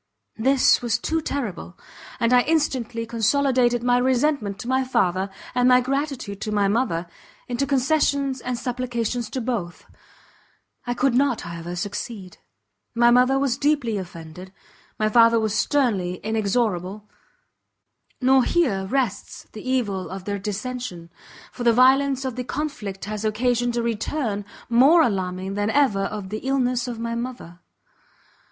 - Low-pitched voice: No, high, 235 Hz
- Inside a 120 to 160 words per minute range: Yes, average, 145 wpm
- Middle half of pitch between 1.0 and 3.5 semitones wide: No, average, 4.2 semitones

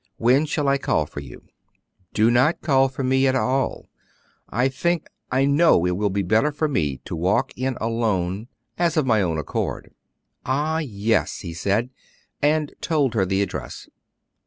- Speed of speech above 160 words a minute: Yes, average, 170 wpm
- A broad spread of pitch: Yes, wide, 6.0 semitones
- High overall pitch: No, low, 125 Hz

